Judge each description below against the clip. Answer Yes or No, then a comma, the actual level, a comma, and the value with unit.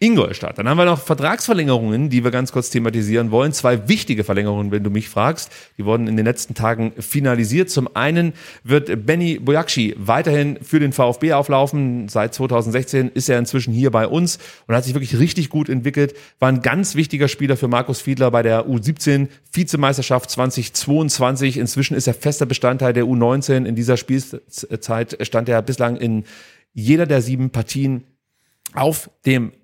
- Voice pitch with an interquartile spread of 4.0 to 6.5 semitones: No, average, 3.5 semitones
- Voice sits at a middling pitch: No, low, 130 Hz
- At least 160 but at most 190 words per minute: Yes, average, 170 wpm